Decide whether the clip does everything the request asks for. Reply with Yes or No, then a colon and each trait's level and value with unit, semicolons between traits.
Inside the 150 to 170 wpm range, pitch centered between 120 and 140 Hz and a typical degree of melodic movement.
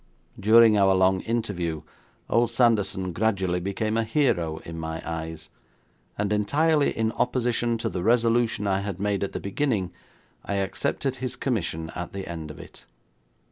No: average, 155 wpm; low, 100 Hz; average, 4.5 semitones